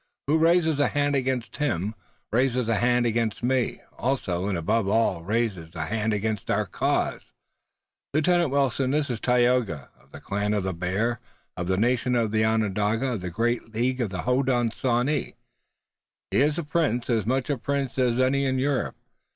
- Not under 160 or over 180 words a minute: Yes, average, 170 wpm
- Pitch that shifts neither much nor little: Yes, average, 3.9 semitones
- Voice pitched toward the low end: Yes, low, 120 Hz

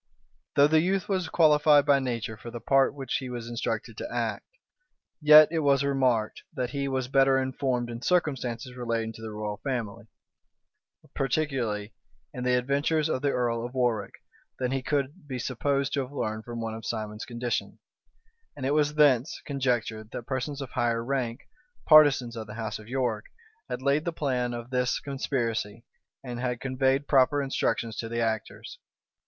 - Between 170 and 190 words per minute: Yes, average, 175 wpm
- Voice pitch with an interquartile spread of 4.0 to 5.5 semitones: No, average, 3.2 semitones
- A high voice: No, low, 130 Hz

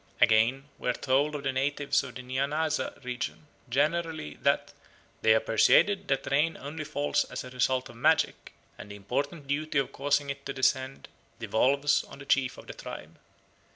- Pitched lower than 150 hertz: Yes, medium, 140 Hz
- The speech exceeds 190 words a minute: No, average, 180 wpm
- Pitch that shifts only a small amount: Yes, narrow, 2.3 semitones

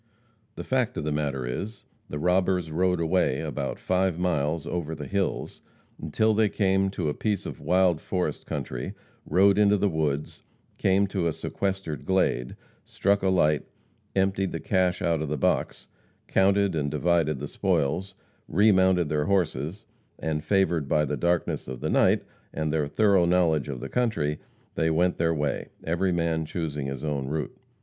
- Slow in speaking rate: No, average, 170 wpm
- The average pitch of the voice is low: Yes, very low, 85 Hz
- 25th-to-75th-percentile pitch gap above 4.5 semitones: No, average, 4.1 semitones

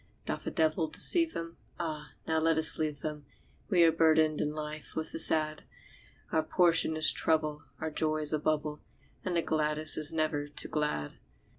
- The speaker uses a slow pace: No, average, 180 wpm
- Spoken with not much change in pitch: Yes, narrow, 1.1 semitones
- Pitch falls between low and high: Yes, medium, 155 Hz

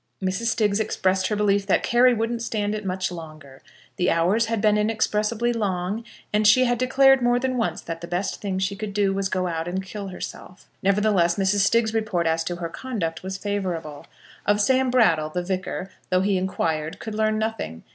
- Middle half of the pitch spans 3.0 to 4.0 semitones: Yes, average, 3.4 semitones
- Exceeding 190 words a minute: Yes, average, 200 wpm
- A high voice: Yes, high, 200 Hz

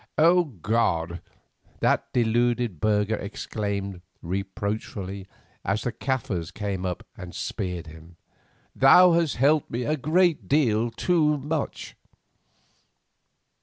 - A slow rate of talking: Yes, slow, 100 wpm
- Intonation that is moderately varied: No, wide, 6.4 semitones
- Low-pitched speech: Yes, low, 110 Hz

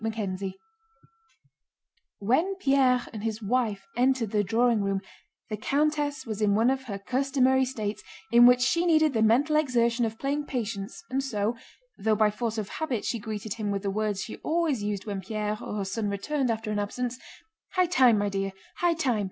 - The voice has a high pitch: Yes, high, 230 Hz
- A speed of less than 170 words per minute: No, average, 185 wpm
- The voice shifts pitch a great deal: No, average, 4.3 semitones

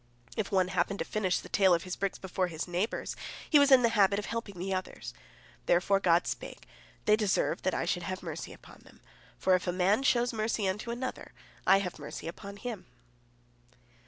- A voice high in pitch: Yes, high, 195 Hz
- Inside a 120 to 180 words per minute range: No, average, 200 wpm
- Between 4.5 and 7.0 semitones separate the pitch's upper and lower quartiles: No, average, 2.9 semitones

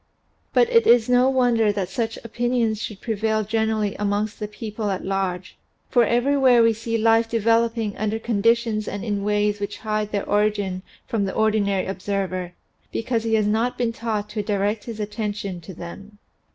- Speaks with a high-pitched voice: Yes, high, 215 Hz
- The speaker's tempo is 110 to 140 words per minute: No, average, 170 wpm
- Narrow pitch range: Yes, narrow, 2.1 semitones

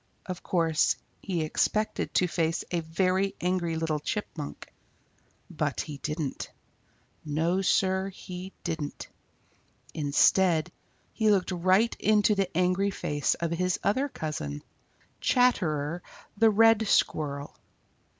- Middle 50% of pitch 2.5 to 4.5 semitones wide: Yes, average, 3.6 semitones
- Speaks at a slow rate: Yes, slow, 110 wpm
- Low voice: No, medium, 180 Hz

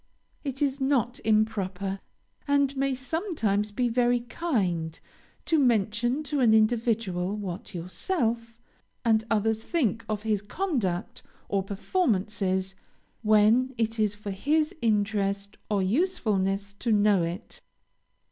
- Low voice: No, high, 220 Hz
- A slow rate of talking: Yes, slow, 120 wpm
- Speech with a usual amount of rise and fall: Yes, average, 4.3 semitones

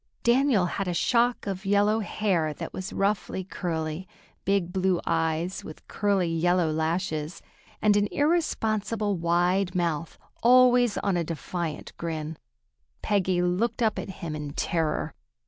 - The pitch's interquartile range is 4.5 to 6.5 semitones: No, average, 3.7 semitones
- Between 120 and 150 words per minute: Yes, slow, 135 wpm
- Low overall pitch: No, medium, 185 Hz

